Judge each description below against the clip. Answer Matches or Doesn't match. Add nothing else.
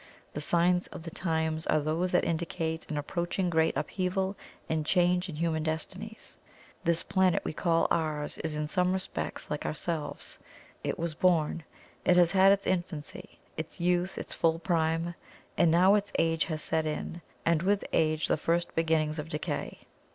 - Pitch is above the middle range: Doesn't match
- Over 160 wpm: Matches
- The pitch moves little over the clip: Matches